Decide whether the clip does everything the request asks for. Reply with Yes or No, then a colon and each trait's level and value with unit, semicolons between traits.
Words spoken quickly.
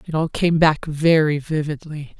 No: average, 165 wpm